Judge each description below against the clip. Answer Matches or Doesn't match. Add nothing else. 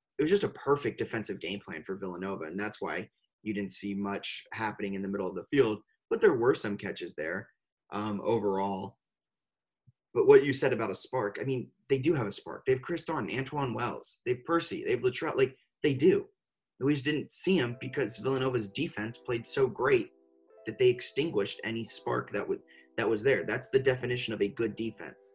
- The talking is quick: Matches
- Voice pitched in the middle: Doesn't match